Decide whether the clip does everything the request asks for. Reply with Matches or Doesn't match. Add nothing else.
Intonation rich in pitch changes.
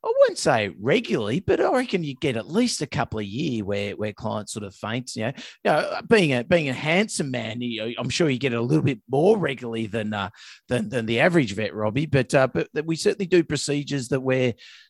Matches